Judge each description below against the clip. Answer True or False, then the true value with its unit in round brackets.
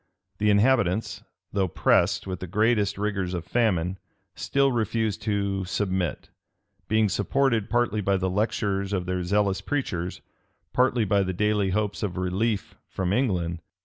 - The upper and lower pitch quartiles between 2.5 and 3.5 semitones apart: True (2.9 semitones)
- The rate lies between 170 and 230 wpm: False (145 wpm)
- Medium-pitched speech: False (100 Hz)